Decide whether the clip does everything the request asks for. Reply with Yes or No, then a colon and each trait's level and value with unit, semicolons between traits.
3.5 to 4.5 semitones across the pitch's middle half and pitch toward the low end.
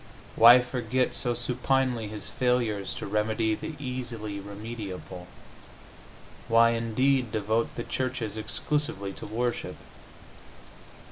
No: average, 2.8 semitones; low, 115 Hz